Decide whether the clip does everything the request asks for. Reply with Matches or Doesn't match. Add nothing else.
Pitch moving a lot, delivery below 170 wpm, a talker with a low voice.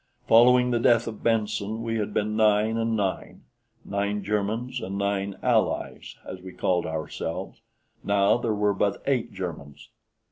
Doesn't match